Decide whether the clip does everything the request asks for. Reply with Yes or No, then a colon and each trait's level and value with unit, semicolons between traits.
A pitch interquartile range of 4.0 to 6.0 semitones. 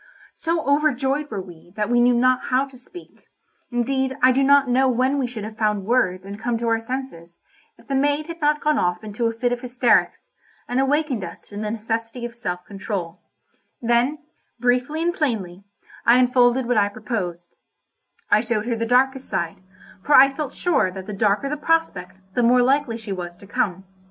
Yes: average, 4.3 semitones